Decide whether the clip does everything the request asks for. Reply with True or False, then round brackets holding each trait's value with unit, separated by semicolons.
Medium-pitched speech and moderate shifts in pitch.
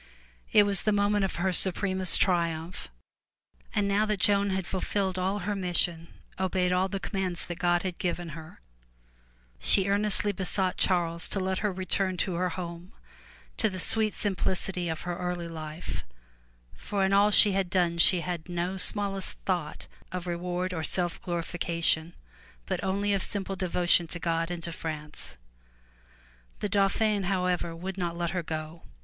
False (180 Hz; 2.2 semitones)